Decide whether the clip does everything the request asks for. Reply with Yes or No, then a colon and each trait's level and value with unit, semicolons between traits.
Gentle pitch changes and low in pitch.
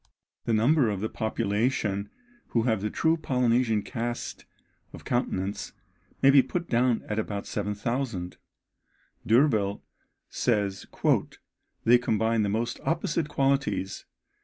No: average, 3.7 semitones; low, 115 Hz